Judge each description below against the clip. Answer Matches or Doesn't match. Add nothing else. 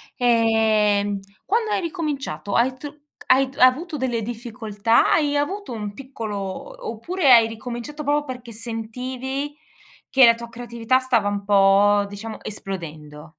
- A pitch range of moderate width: Matches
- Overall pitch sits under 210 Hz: Doesn't match